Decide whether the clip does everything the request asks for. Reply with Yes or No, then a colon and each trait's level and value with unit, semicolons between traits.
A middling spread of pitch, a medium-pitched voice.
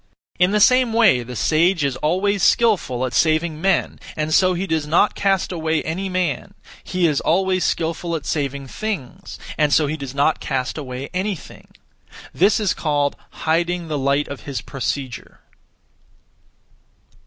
Yes: average, 4.7 semitones; medium, 160 Hz